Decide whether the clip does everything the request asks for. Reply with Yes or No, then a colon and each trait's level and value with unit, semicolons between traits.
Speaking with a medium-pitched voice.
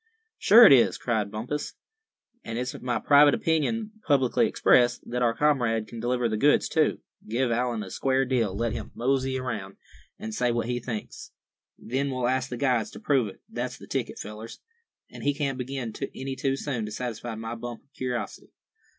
No: low, 125 Hz